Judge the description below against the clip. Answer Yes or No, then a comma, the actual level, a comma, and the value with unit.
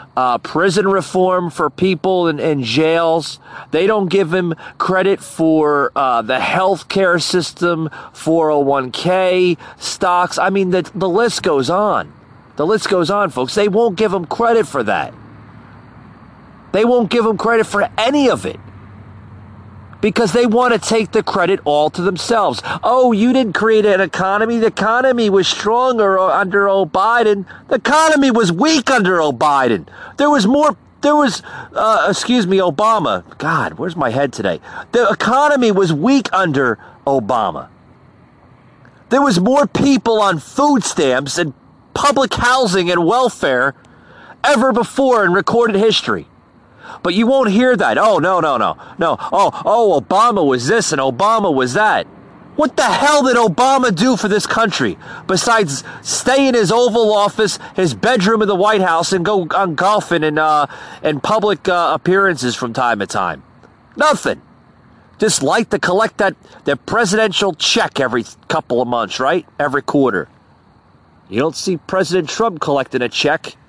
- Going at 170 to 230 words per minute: No, average, 155 wpm